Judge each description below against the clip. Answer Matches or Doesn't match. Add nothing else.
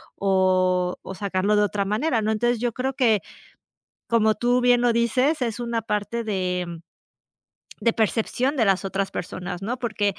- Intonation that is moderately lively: Matches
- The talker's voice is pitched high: Matches